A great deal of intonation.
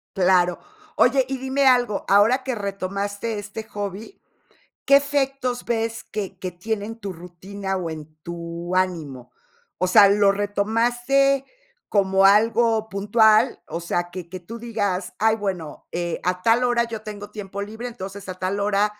No: average, 3.6 semitones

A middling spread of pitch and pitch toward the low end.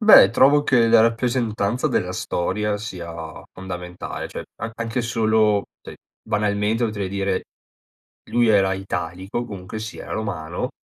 Yes: average, 3.2 semitones; low, 105 Hz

